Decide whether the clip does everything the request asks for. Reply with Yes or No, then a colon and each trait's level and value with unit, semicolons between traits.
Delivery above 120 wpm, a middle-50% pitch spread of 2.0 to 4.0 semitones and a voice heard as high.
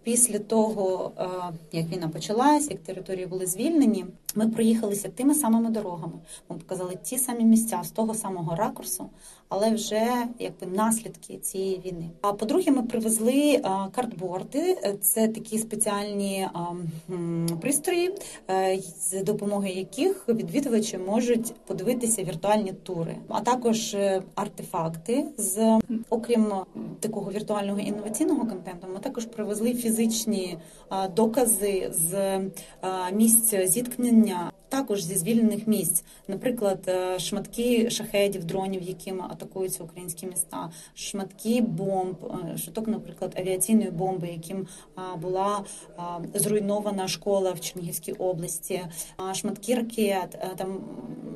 No: slow, 105 wpm; average, 3.3 semitones; high, 200 Hz